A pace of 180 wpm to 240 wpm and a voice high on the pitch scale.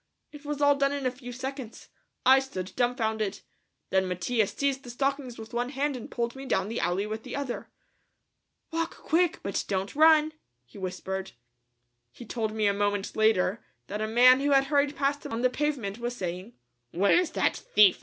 Yes: average, 190 wpm; high, 240 Hz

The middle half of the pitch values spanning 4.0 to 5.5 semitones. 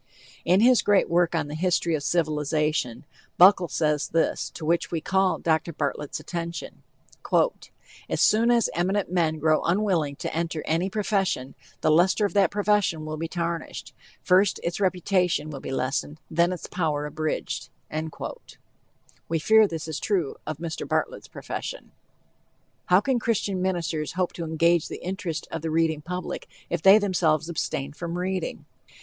No: average, 3.3 semitones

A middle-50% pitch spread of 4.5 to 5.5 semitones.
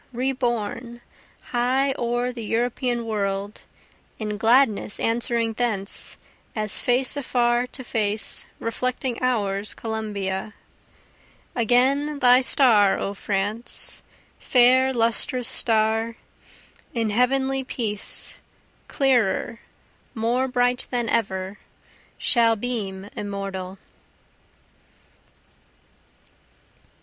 No: average, 3.0 semitones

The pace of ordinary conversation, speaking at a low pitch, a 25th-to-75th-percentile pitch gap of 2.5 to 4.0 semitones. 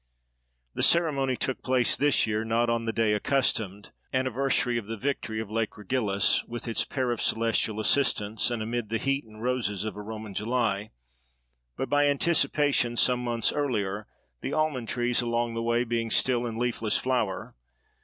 Yes: average, 165 wpm; low, 120 Hz; average, 2.8 semitones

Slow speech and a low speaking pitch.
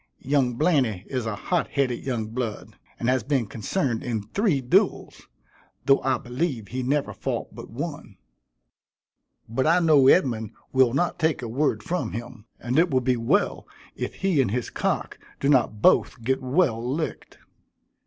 No: average, 165 wpm; low, 130 Hz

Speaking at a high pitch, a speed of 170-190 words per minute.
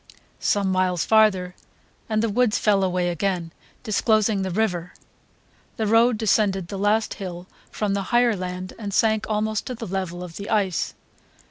No: high, 200 Hz; average, 160 wpm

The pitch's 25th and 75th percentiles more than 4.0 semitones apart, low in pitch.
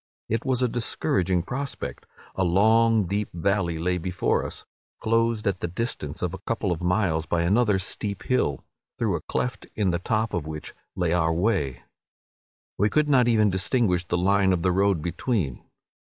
Yes: average, 4.5 semitones; very low, 95 Hz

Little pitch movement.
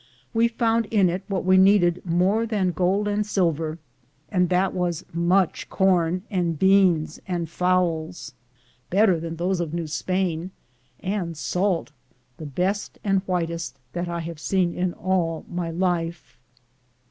Yes: narrow, 2.3 semitones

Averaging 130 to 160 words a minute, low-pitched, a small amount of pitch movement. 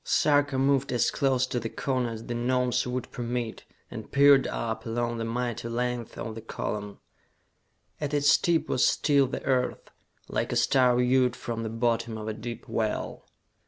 No: average, 175 wpm; low, 125 Hz; narrow, 2.3 semitones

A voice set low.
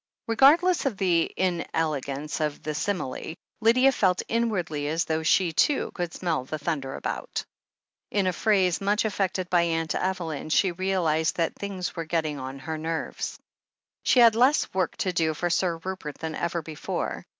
No: medium, 170 Hz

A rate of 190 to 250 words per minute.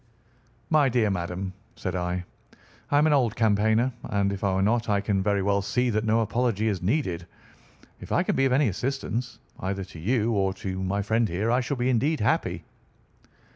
Yes: average, 200 wpm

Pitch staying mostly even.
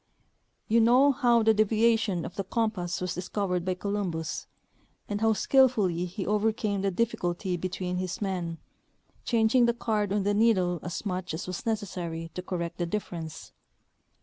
No: average, 3.7 semitones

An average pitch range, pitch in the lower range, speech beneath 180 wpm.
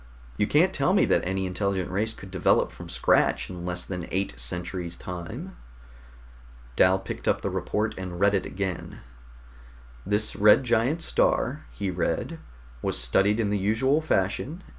Yes: average, 3.5 semitones; low, 100 Hz; average, 160 wpm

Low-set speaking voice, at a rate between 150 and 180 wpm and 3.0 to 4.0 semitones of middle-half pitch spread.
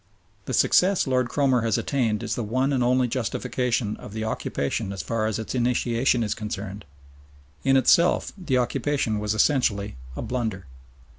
Yes: low, 120 Hz; average, 160 wpm; average, 3.3 semitones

